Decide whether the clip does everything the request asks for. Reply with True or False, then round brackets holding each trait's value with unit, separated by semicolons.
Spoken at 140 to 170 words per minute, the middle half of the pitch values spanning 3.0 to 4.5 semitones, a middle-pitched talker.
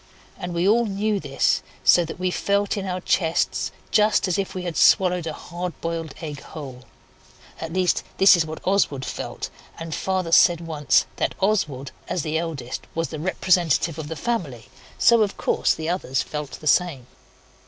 False (180 wpm; 3.4 semitones; 170 Hz)